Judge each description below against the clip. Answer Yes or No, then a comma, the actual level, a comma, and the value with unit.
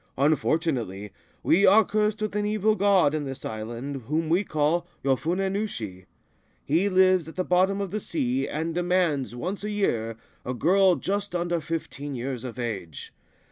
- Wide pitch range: Yes, wide, 6.7 semitones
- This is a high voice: No, medium, 165 Hz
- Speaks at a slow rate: No, average, 165 wpm